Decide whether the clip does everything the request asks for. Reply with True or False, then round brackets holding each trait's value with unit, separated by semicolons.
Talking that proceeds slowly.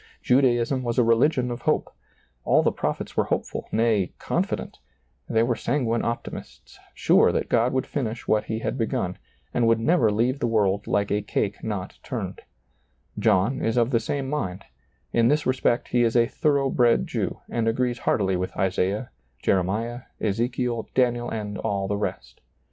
False (170 wpm)